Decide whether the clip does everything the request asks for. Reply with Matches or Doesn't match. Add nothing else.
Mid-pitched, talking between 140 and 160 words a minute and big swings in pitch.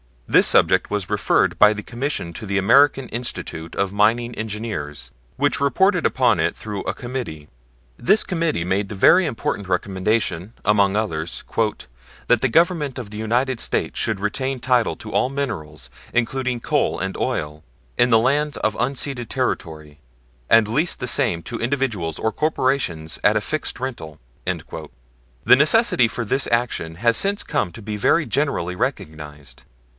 Doesn't match